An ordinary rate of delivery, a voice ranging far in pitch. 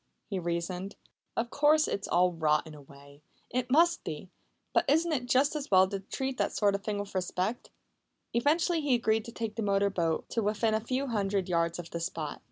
No: fast, 210 wpm; wide, 6.1 semitones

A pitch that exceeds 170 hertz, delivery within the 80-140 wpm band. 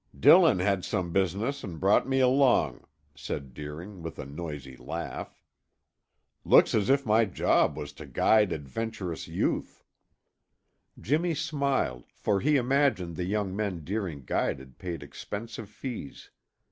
No: very low, 95 Hz; slow, 135 wpm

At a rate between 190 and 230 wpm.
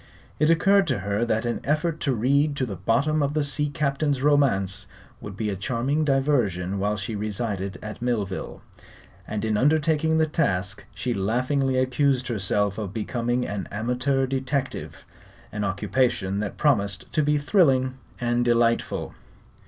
No: average, 150 wpm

